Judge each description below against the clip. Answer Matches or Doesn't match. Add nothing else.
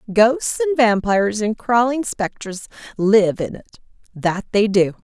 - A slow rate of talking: Matches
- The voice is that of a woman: Matches